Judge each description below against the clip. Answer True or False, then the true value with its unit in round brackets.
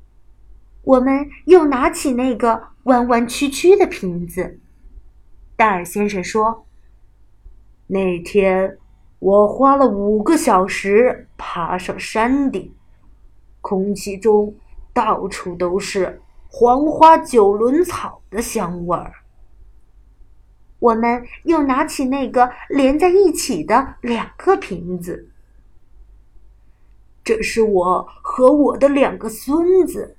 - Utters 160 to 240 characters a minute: False (145 characters per minute)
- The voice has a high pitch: True (205 Hz)